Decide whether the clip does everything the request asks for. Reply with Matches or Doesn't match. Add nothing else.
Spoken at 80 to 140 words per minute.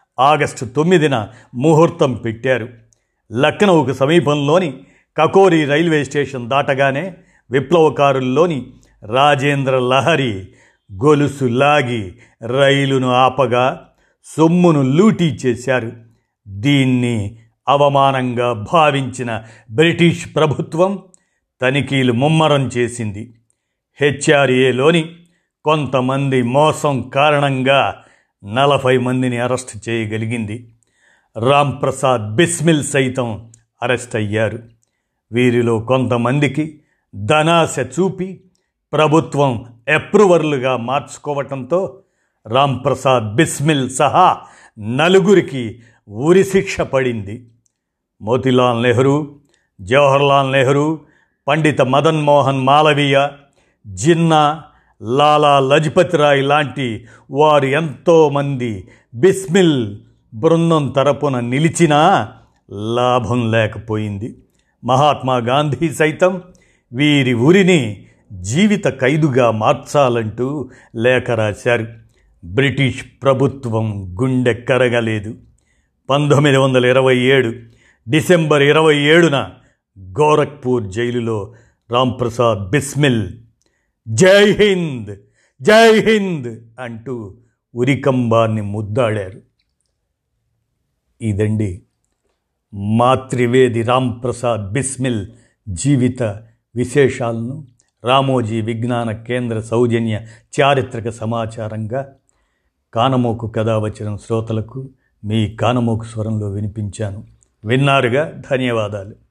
Doesn't match